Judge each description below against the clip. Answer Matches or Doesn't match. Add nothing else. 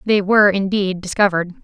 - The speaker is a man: Doesn't match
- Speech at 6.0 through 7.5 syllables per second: Matches